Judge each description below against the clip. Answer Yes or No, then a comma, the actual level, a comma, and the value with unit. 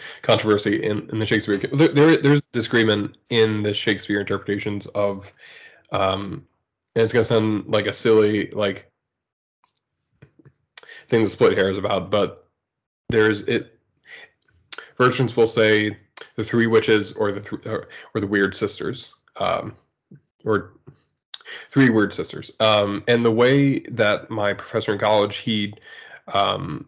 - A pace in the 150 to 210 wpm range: No, average, 140 wpm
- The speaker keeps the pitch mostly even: Yes, narrow, 2.1 semitones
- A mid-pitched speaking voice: No, low, 110 Hz